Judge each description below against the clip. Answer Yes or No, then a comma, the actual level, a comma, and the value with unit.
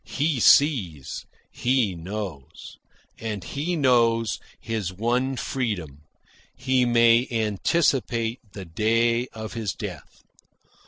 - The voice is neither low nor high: No, low, 115 Hz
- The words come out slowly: Yes, slow, 100 wpm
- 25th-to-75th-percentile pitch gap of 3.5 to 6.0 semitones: Yes, average, 3.8 semitones